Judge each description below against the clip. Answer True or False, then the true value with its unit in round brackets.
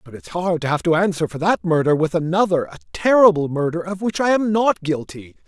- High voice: False (175 Hz)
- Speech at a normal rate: False (230 wpm)